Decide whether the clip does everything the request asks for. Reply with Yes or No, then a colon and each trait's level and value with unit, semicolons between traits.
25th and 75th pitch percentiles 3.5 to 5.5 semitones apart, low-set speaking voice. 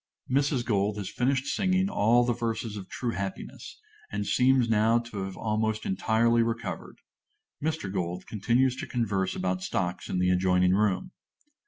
Yes: average, 4.0 semitones; low, 110 Hz